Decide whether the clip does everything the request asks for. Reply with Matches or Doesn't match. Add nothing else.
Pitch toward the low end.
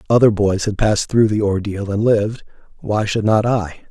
Matches